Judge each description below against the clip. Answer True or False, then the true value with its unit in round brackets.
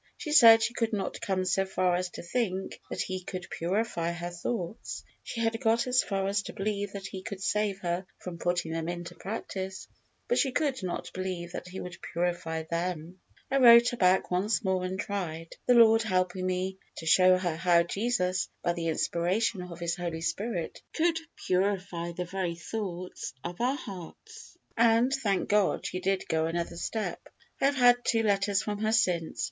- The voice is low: False (190 Hz)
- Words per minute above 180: True (190 wpm)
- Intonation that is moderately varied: True (4.1 semitones)